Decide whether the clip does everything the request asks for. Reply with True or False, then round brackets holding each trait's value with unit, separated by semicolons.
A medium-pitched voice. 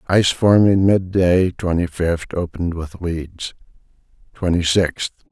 False (90 Hz)